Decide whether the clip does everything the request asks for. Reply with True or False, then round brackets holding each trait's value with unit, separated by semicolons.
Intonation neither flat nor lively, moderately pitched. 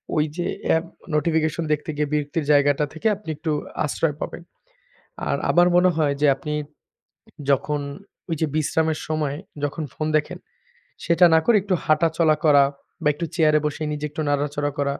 False (1.8 semitones; 155 Hz)